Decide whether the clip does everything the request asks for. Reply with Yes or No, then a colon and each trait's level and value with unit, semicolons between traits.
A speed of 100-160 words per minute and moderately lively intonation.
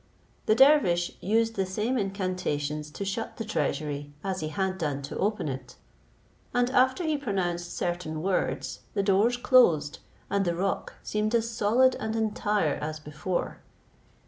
No: average, 150 wpm; wide, 5.9 semitones